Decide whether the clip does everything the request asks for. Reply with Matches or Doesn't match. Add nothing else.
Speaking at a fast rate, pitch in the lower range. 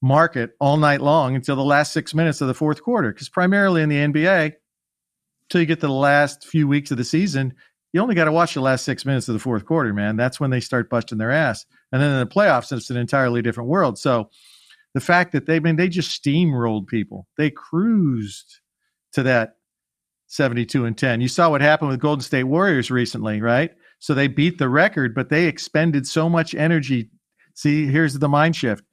Doesn't match